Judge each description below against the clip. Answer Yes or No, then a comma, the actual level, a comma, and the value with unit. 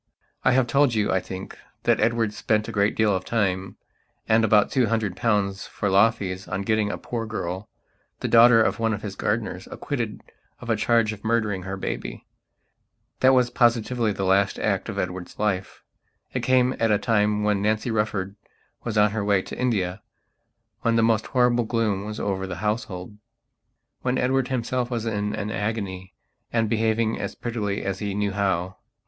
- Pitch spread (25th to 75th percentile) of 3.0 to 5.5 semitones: No, narrow, 2.6 semitones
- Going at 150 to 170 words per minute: No, average, 185 wpm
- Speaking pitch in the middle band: No, low, 105 Hz